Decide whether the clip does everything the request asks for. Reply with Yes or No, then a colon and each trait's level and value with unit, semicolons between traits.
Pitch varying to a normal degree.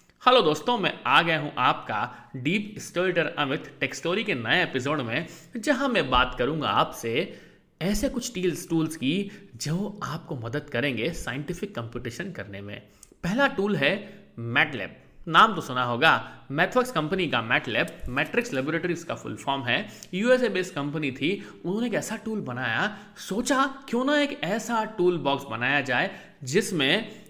No: wide, 6.8 semitones